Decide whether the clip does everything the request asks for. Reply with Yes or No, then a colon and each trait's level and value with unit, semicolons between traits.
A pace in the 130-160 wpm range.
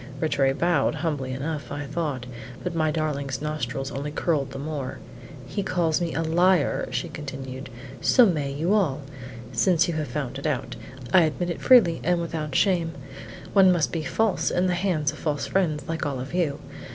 No: average, 185 wpm